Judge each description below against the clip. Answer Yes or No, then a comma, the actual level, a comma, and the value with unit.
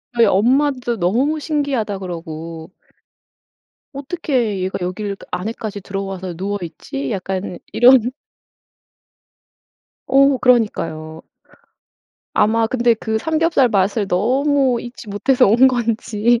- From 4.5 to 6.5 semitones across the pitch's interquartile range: Yes, average, 5.1 semitones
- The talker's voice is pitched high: Yes, high, 220 Hz